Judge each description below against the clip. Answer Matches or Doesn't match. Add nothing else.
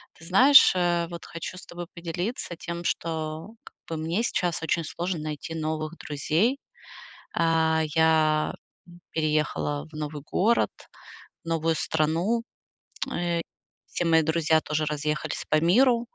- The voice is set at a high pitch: Doesn't match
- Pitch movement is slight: Matches